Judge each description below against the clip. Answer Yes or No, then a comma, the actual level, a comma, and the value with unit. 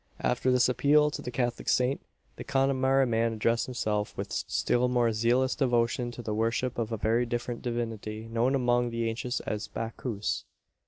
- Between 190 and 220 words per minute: No, average, 170 wpm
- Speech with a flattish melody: Yes, narrow, 1.8 semitones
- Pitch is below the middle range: Yes, low, 120 Hz